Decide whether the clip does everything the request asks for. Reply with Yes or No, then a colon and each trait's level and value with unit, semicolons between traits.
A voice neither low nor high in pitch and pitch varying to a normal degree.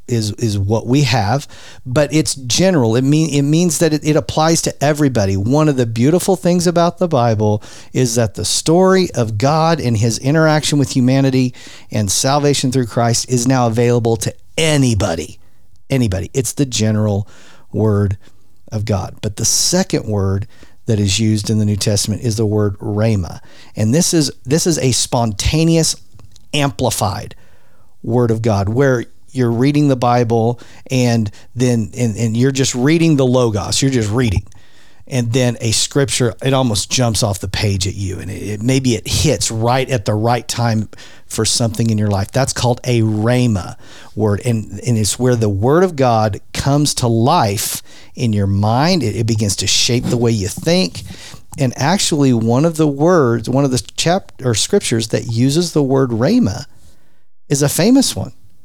No: low, 120 Hz; average, 4.4 semitones